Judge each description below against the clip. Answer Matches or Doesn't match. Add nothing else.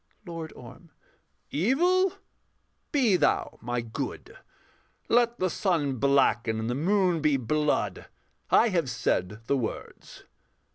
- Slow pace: Matches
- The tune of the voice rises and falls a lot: Matches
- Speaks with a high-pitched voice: Doesn't match